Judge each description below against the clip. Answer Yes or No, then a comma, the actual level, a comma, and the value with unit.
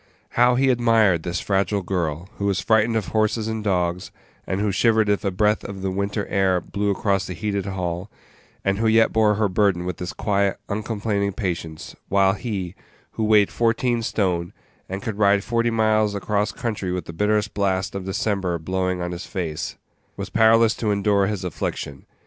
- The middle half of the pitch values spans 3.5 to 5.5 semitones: No, average, 2.7 semitones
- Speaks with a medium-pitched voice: No, low, 100 Hz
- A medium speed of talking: Yes, average, 185 wpm